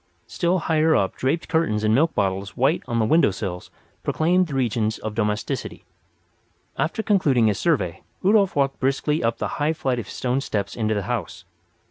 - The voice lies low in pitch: Yes, low, 130 Hz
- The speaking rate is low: No, average, 175 wpm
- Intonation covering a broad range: Yes, wide, 7.0 semitones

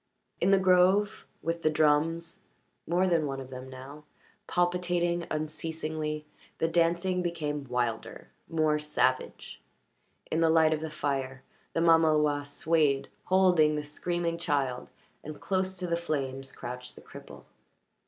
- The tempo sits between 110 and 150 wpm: Yes, slow, 135 wpm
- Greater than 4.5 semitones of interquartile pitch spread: No, average, 3.0 semitones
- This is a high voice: No, medium, 155 Hz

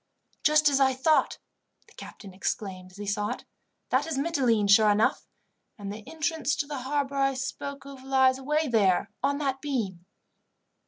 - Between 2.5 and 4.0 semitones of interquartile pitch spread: No, wide, 5.4 semitones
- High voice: Yes, very high, 265 Hz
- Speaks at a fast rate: No, average, 170 wpm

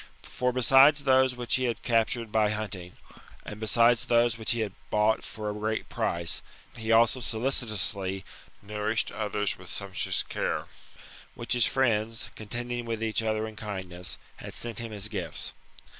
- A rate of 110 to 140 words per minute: No, average, 160 wpm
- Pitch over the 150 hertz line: No, low, 110 Hz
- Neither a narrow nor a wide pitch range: No, narrow, 2.2 semitones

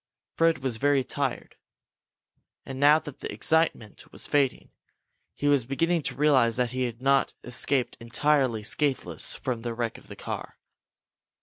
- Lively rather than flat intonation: No, average, 3.0 semitones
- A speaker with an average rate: Yes, average, 150 wpm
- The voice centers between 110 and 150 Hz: Yes, low, 135 Hz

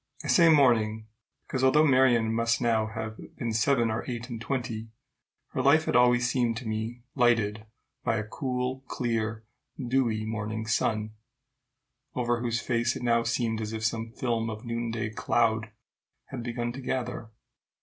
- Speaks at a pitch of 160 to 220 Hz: No, low, 115 Hz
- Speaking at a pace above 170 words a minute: No, average, 160 wpm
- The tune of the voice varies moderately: No, narrow, 1.9 semitones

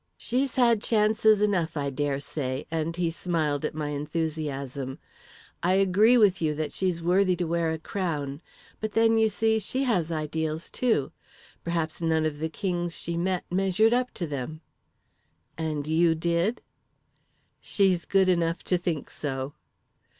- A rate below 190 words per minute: Yes, average, 155 wpm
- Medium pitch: Yes, medium, 170 Hz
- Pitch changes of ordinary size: Yes, average, 4.0 semitones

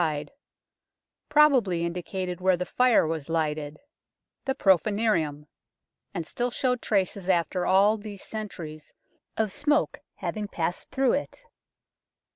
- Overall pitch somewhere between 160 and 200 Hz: Yes, high, 190 Hz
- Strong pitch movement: No, average, 4.9 semitones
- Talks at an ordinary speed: No, slow, 125 wpm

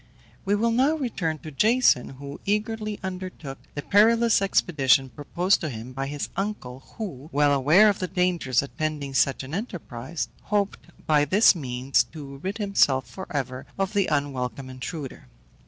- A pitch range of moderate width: No, wide, 6.8 semitones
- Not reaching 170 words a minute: Yes, average, 155 wpm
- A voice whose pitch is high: No, medium, 155 Hz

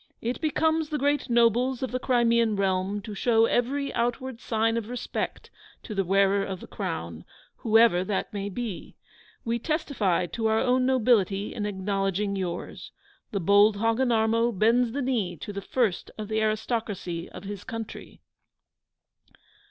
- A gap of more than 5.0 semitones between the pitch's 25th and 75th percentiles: No, average, 3.5 semitones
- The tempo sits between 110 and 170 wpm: Yes, average, 150 wpm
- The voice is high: Yes, high, 220 Hz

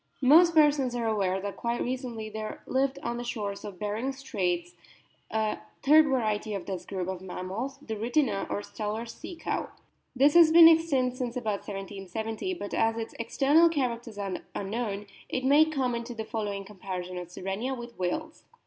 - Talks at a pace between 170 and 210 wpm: Yes, average, 175 wpm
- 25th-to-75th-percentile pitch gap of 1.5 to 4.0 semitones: No, average, 4.9 semitones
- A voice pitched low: No, high, 230 Hz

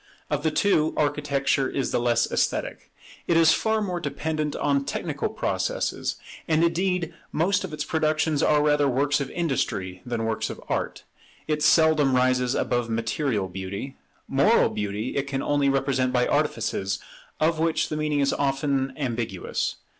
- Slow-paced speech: No, average, 155 wpm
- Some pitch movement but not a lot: Yes, average, 3.6 semitones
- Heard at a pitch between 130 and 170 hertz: Yes, medium, 140 Hz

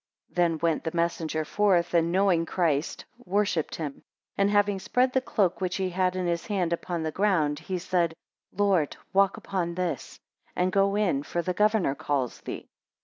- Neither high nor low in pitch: Yes, medium, 180 Hz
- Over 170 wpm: Yes, average, 180 wpm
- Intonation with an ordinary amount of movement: Yes, average, 3.0 semitones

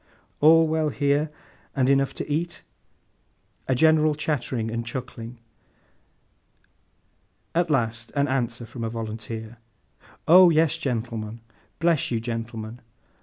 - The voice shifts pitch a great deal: No, average, 5.0 semitones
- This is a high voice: No, low, 130 Hz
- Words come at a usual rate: No, slow, 115 wpm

